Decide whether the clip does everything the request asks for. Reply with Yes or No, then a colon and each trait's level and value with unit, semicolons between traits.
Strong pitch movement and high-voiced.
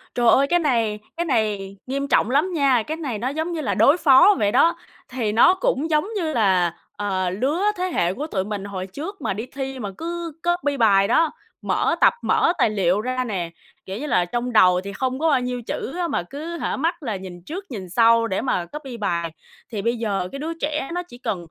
Yes: wide, 7.4 semitones; very high, 250 Hz